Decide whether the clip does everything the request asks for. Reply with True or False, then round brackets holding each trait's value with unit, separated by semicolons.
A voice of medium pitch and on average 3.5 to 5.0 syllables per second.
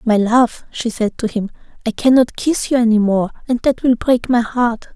False (235 Hz; 4.8 syllables/s)